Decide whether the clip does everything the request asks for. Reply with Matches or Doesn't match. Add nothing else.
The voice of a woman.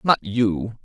Doesn't match